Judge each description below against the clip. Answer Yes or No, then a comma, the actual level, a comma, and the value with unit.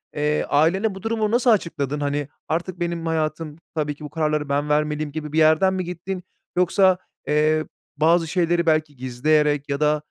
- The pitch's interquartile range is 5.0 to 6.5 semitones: No, average, 2.7 semitones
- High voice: No, medium, 155 Hz